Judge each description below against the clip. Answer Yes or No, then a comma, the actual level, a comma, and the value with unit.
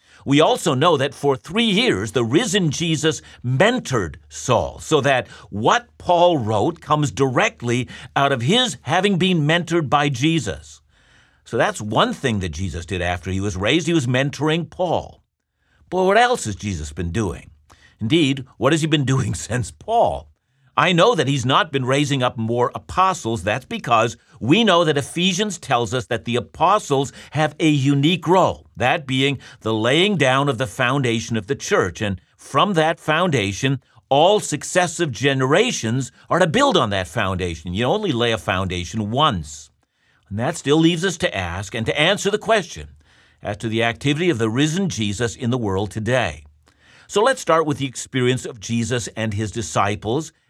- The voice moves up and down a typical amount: No, wide, 6.7 semitones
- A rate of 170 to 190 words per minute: Yes, average, 175 wpm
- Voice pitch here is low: Yes, low, 130 Hz